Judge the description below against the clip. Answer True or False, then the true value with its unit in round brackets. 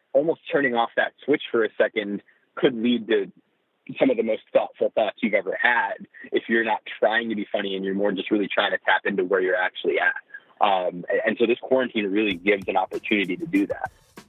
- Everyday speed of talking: False (220 wpm)